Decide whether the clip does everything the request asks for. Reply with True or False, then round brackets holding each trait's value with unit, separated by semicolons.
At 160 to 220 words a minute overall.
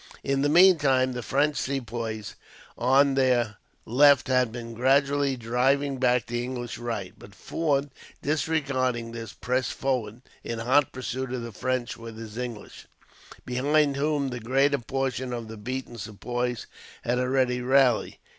False (145 wpm)